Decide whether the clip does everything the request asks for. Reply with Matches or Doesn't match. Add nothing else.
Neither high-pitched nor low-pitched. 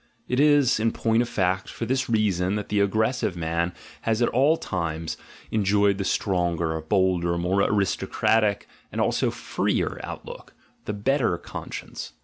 Doesn't match